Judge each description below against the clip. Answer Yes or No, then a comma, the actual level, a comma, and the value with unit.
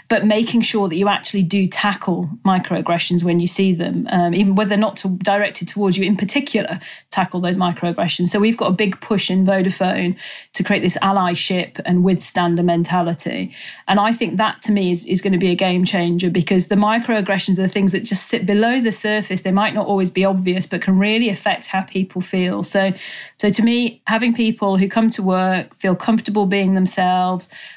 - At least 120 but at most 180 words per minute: No, fast, 205 wpm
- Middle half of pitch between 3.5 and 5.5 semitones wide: No, narrow, 2.4 semitones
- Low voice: No, high, 195 Hz